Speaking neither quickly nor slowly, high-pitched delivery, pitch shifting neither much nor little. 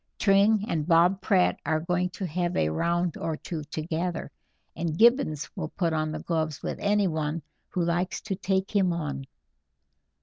No: average, 165 wpm; medium, 170 Hz; average, 3.2 semitones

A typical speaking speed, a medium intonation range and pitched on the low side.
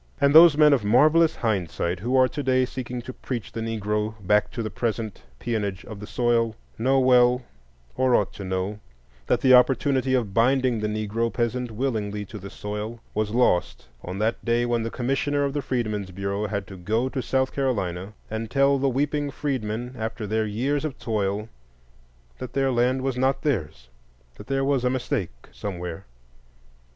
Yes: average, 175 wpm; average, 3.8 semitones; low, 115 Hz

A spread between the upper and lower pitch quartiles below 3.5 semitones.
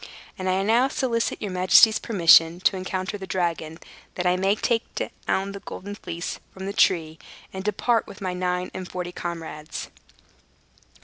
Yes: narrow, 2.4 semitones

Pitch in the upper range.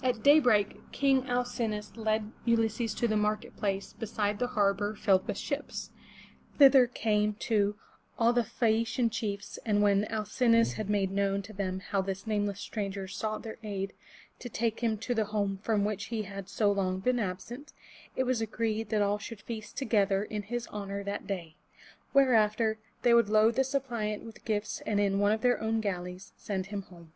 Yes: high, 215 Hz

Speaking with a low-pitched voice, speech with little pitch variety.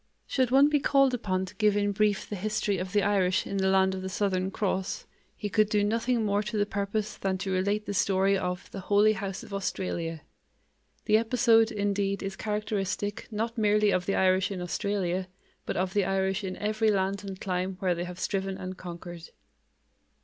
No: high, 200 Hz; narrow, 2.0 semitones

